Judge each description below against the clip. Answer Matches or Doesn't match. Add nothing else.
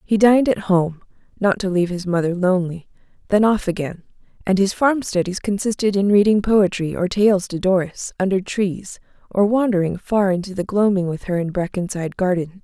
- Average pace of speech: Matches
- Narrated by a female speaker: Matches